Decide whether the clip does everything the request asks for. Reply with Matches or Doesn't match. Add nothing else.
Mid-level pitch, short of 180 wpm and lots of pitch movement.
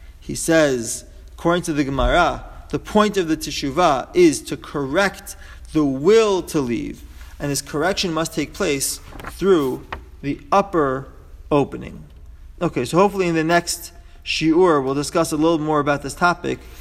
Matches